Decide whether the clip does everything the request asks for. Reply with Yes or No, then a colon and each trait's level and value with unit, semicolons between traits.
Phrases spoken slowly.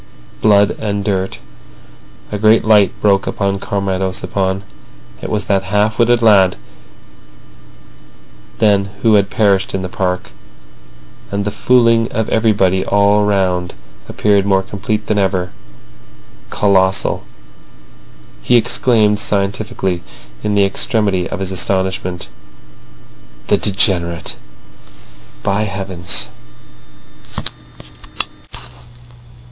Yes: slow, 95 wpm